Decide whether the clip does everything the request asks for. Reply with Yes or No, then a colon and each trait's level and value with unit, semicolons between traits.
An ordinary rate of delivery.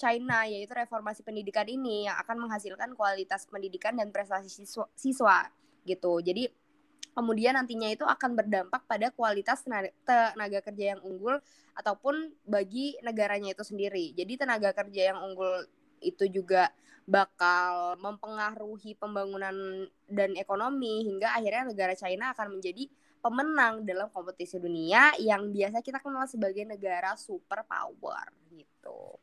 Yes: average, 130 wpm